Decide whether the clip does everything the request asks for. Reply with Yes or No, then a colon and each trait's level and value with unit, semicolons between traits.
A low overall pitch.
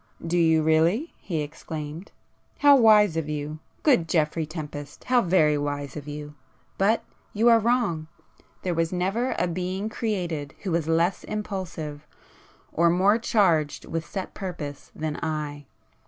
No: medium, 165 Hz